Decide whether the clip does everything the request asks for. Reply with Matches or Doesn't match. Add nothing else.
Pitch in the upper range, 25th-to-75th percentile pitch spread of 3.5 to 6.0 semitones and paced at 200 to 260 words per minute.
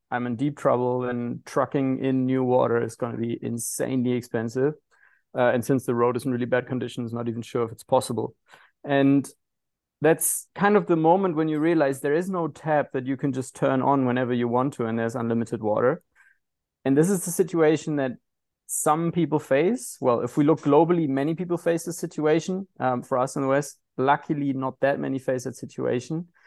Doesn't match